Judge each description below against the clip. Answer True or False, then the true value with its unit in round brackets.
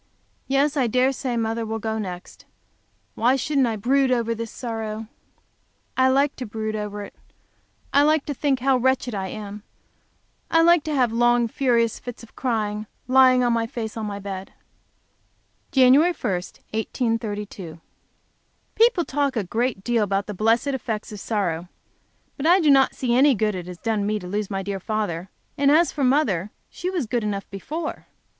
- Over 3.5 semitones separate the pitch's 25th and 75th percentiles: True (4.2 semitones)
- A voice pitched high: True (230 Hz)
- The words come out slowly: False (175 wpm)